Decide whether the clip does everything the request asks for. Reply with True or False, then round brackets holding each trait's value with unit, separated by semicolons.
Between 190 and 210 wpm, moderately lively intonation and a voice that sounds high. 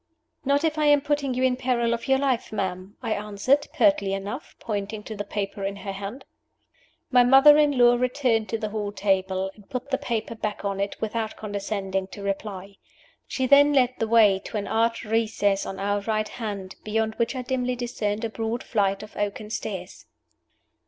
True (195 wpm; 3.9 semitones; 220 Hz)